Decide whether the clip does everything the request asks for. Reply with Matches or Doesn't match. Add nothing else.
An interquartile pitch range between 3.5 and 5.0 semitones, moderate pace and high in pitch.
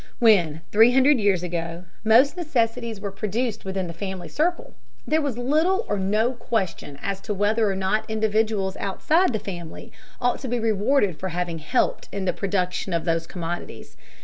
Matches